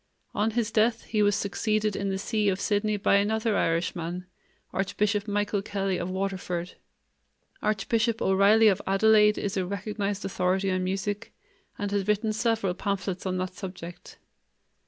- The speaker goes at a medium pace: Yes, average, 150 wpm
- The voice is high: Yes, high, 200 Hz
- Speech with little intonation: Yes, narrow, 2.0 semitones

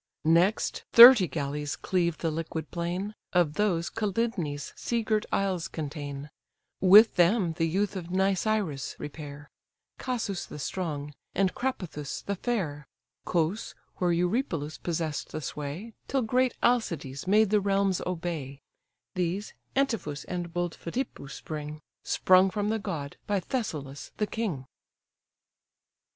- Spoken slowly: Yes, slow, 125 wpm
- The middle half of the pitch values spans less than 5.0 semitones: No, average, 5.3 semitones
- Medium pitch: Yes, medium, 175 Hz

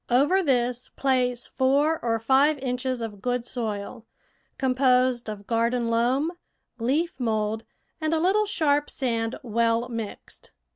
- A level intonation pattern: No, average, 3.1 semitones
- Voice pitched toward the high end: Yes, very high, 250 Hz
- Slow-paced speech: Yes, slow, 130 wpm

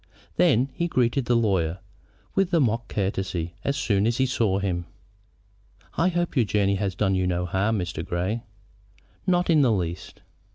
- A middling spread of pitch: No, wide, 5.7 semitones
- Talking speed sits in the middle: Yes, average, 170 wpm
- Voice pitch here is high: No, low, 105 Hz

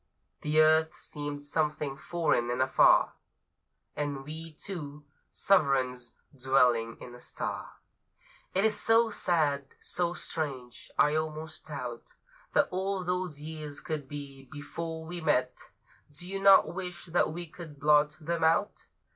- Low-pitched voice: No, medium, 155 Hz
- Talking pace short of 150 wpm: Yes, slow, 135 wpm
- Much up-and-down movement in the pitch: No, average, 3.5 semitones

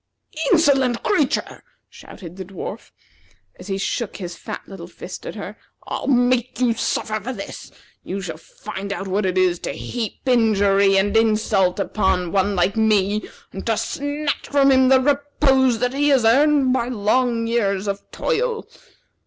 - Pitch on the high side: Yes, high, 225 Hz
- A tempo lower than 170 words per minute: Yes, average, 160 wpm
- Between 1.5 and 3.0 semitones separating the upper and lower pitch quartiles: No, average, 4.9 semitones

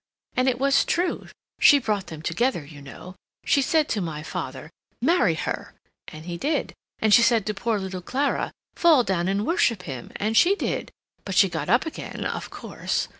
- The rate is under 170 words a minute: No, average, 190 wpm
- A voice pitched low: No, high, 210 Hz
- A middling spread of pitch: No, wide, 7.3 semitones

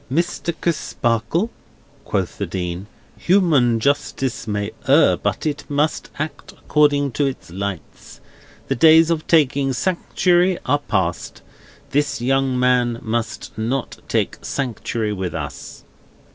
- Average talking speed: No, slow, 120 wpm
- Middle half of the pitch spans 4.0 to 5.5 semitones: Yes, average, 5.2 semitones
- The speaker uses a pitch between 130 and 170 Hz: Yes, low, 135 Hz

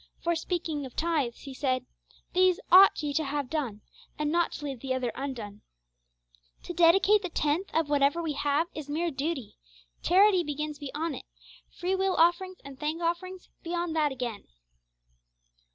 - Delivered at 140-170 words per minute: Yes, average, 165 wpm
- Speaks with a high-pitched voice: Yes, very high, 310 Hz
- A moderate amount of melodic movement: Yes, average, 3.7 semitones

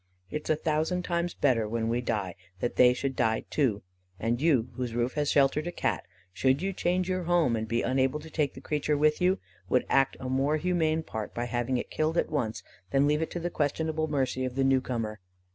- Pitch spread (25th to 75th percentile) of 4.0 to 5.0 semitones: Yes, average, 4.5 semitones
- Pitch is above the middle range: No, low, 135 Hz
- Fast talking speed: Yes, fast, 230 wpm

